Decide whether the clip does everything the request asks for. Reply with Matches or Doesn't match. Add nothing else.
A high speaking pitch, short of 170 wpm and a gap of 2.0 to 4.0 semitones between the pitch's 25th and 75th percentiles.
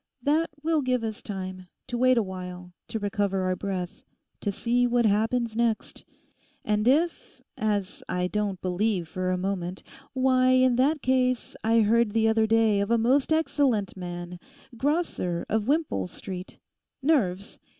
Doesn't match